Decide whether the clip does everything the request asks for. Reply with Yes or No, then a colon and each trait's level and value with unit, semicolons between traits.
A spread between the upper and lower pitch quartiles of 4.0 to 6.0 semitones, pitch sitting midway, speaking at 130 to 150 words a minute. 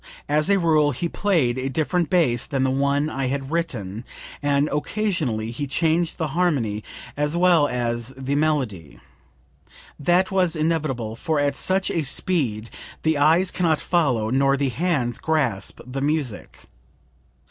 Yes: average, 4.6 semitones; medium, 145 Hz; average, 145 wpm